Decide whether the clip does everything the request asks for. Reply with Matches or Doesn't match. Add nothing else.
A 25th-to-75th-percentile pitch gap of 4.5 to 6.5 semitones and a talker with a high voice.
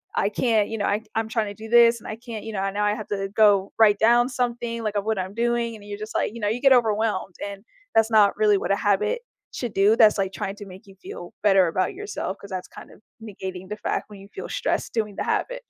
Doesn't match